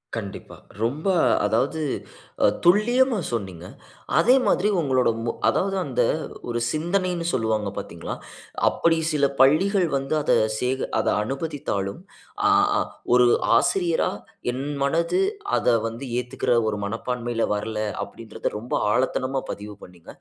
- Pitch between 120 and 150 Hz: Yes, low, 135 Hz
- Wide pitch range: Yes, wide, 6.7 semitones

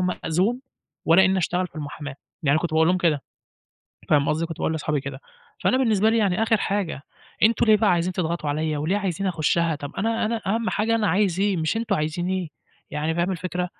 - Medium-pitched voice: Yes, medium, 180 Hz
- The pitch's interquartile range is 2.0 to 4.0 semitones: No, average, 4.4 semitones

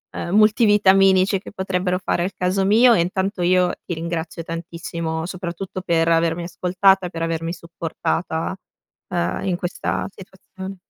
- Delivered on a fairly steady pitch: Yes, narrow, 2.3 semitones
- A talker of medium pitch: Yes, medium, 180 Hz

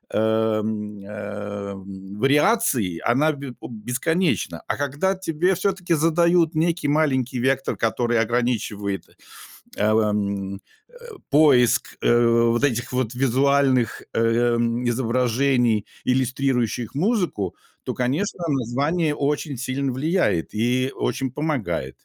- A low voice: Yes, low, 125 Hz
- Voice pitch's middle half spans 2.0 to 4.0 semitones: No, average, 4.8 semitones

